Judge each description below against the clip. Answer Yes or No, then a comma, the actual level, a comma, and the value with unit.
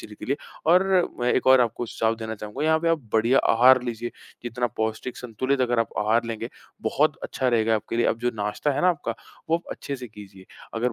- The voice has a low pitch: Yes, low, 120 Hz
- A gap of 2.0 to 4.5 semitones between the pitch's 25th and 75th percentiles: Yes, average, 2.8 semitones